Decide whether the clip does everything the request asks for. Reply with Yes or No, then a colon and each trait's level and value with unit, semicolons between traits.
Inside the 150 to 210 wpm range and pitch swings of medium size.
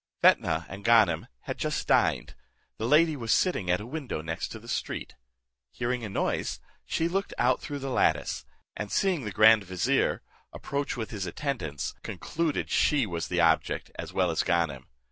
No: average, 170 wpm; wide, 8.0 semitones